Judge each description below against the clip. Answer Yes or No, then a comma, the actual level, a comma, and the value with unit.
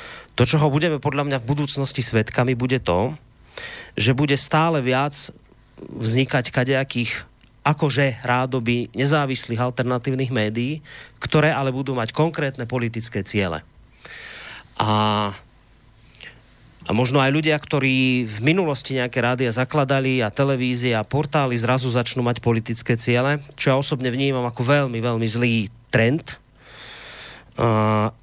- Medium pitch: No, low, 125 Hz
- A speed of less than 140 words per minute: Yes, average, 125 wpm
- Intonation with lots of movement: No, average, 2.7 semitones